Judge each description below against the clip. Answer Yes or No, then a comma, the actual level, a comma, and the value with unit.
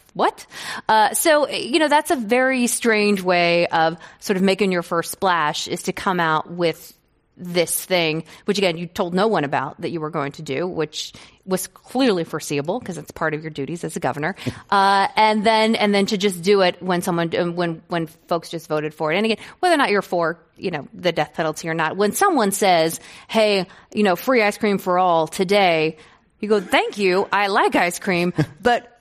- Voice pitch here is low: No, medium, 180 Hz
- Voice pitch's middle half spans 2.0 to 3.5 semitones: No, average, 4.2 semitones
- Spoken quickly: Yes, fast, 215 wpm